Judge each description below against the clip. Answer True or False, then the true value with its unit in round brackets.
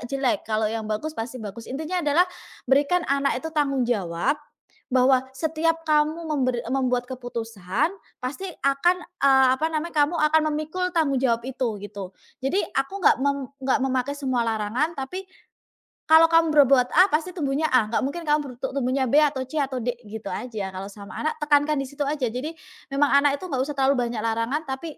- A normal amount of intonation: True (3.8 semitones)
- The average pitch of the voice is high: True (275 Hz)